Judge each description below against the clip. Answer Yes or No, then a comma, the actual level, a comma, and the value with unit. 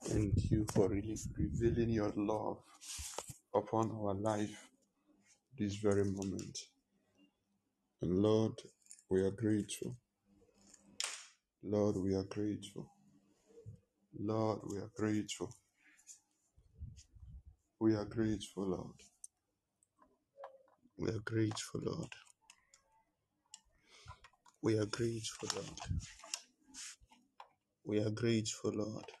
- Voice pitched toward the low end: Yes, low, 105 Hz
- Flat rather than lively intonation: Yes, narrow, 1.7 semitones